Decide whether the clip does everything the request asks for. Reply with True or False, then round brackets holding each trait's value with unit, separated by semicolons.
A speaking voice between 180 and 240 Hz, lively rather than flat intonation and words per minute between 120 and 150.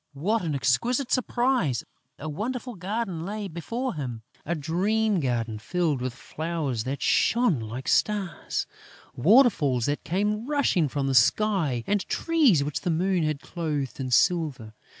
False (170 Hz; 7.5 semitones; 145 wpm)